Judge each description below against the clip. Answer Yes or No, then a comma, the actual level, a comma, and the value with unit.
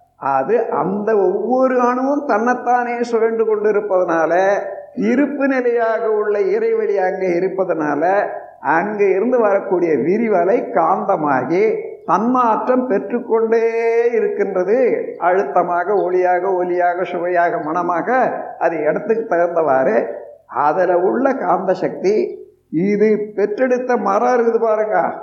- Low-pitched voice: No, high, 225 Hz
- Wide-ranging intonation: Yes, wide, 5.8 semitones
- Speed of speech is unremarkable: Yes, average, 95 wpm